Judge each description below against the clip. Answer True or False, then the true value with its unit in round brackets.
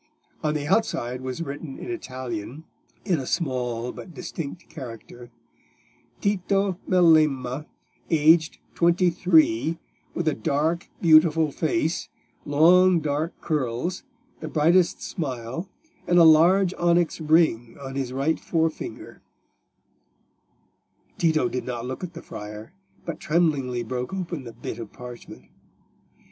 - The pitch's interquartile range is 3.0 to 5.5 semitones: True (5.0 semitones)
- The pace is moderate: False (120 wpm)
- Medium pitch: True (155 Hz)